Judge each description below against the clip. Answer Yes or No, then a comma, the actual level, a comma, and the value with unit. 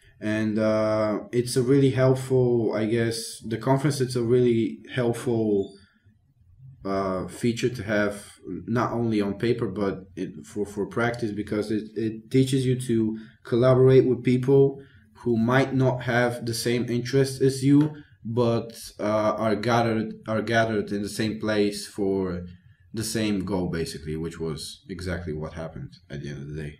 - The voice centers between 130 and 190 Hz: No, low, 110 Hz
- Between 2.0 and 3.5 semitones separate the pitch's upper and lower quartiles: Yes, average, 3.2 semitones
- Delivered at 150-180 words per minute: Yes, average, 160 wpm